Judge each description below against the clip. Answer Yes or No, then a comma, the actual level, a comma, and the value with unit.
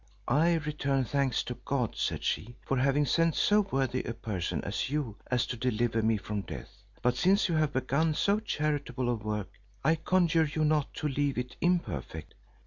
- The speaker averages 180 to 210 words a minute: Yes, average, 185 wpm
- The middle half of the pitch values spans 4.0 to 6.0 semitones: Yes, average, 4.8 semitones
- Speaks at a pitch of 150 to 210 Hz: No, low, 135 Hz